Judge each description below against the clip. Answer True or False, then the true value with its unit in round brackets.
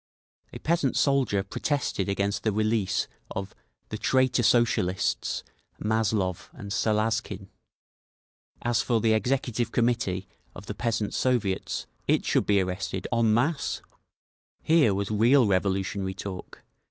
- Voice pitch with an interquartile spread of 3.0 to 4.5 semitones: True (3.4 semitones)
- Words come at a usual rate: False (115 wpm)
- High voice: False (110 Hz)